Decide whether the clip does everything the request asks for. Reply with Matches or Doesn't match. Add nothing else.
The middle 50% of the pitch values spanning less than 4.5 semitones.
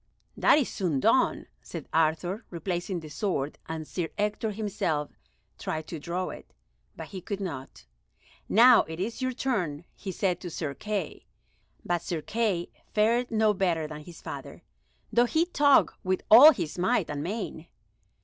Doesn't match